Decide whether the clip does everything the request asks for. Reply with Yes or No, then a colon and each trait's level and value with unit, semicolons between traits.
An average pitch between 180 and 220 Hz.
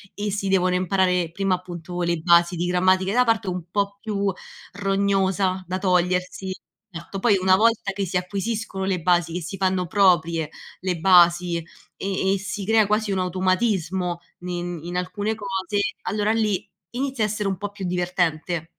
Yes: medium, 185 Hz